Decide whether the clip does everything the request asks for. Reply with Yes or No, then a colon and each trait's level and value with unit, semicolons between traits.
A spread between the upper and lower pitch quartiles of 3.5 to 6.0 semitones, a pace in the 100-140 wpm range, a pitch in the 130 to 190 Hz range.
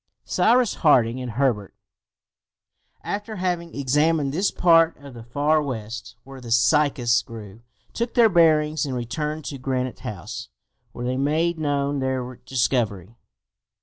Yes: average, 4.7 semitones; slow, 135 wpm; low, 135 Hz